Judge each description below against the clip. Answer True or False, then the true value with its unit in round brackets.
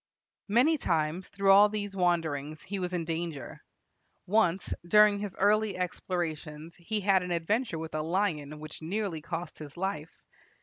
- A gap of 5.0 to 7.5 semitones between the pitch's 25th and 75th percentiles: False (4.1 semitones)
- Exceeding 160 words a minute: False (155 wpm)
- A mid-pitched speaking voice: True (180 Hz)